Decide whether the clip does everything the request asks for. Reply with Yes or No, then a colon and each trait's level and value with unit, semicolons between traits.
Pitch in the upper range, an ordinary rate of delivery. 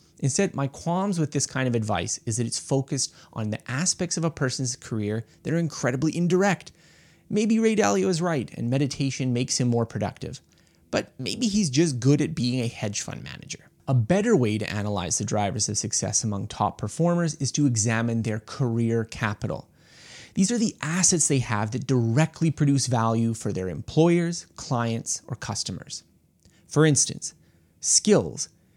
No: low, 135 Hz; average, 170 wpm